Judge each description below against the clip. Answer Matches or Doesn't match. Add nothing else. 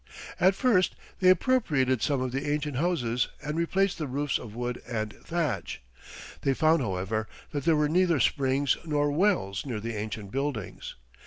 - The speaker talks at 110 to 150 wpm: Doesn't match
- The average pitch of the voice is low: Doesn't match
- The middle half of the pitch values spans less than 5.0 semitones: Doesn't match